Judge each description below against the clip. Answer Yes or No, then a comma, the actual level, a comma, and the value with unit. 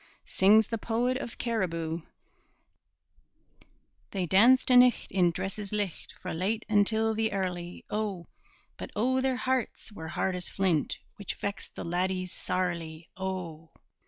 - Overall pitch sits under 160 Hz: No, high, 195 Hz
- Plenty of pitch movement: No, average, 4.0 semitones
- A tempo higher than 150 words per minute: No, slow, 135 wpm